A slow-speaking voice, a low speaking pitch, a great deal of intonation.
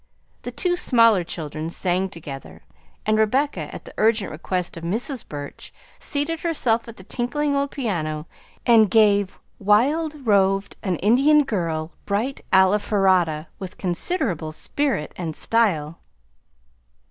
No: slow, 125 wpm; high, 205 Hz; wide, 6.6 semitones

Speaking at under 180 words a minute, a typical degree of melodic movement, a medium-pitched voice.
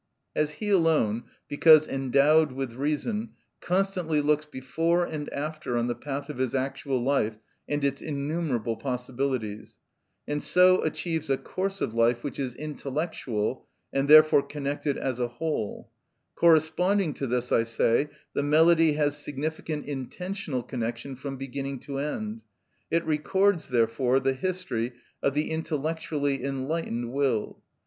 Yes: average, 140 wpm; average, 3.5 semitones; medium, 145 Hz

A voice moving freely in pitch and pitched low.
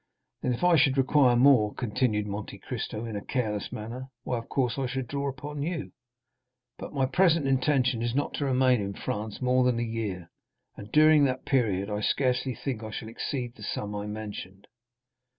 No: average, 4.0 semitones; low, 125 Hz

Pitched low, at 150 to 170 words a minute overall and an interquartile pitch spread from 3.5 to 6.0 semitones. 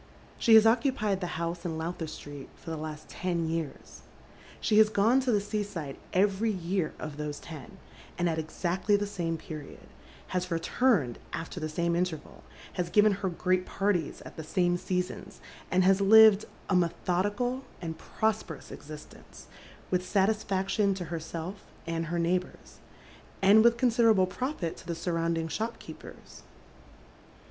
No: medium, 180 Hz; average, 155 wpm; average, 3.8 semitones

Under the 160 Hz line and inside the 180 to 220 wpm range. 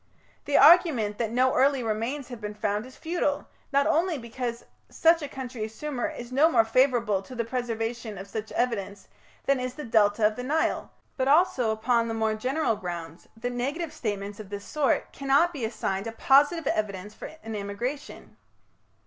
No: high, 240 Hz; average, 185 wpm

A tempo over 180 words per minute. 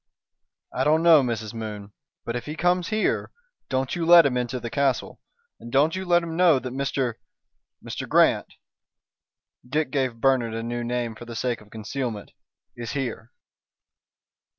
No: average, 165 wpm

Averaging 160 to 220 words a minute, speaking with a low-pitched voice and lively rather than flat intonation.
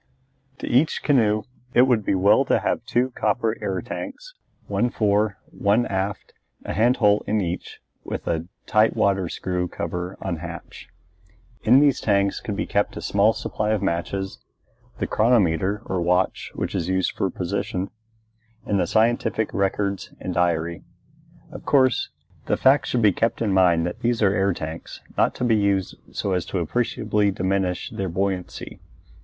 No: average, 165 wpm; low, 100 Hz; average, 3.3 semitones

